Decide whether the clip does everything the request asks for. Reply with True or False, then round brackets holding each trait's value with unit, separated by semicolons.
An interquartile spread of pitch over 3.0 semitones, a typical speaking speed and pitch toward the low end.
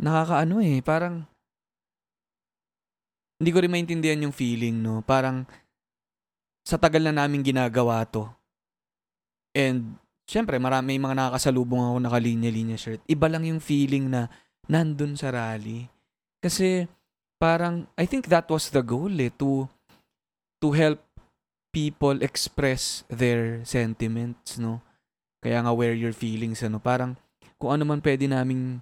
True (4.7 semitones; 130 wpm; 130 Hz)